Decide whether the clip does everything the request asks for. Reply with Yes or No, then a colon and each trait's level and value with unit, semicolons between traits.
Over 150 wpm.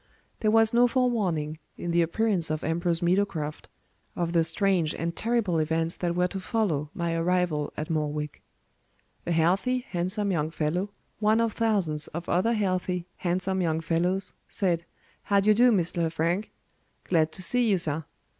Yes: average, 160 wpm